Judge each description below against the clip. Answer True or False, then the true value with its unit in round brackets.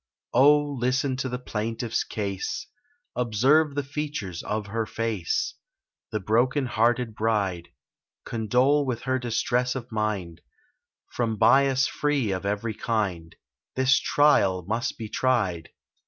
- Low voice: True (115 Hz)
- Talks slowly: True (125 wpm)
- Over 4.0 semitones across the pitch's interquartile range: False (3.7 semitones)